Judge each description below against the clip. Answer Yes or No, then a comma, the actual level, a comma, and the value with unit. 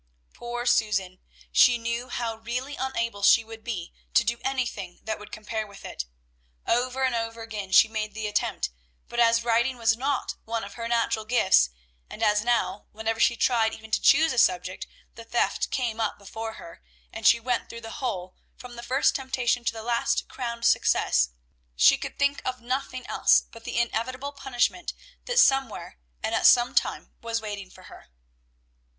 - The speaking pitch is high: Yes, high, 230 Hz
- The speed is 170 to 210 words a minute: Yes, average, 180 wpm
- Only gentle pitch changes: Yes, narrow, 2.2 semitones